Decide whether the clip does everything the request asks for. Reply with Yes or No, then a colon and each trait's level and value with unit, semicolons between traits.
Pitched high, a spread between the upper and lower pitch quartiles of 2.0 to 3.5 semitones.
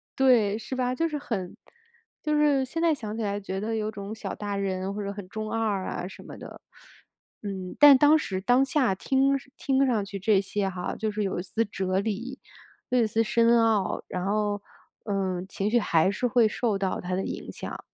No: high, 215 Hz; average, 4.2 semitones